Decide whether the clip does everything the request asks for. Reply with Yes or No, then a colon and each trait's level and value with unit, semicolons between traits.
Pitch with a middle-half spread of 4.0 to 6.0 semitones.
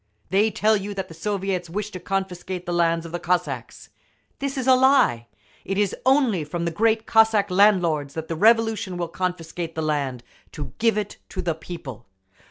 Yes: average, 4.3 semitones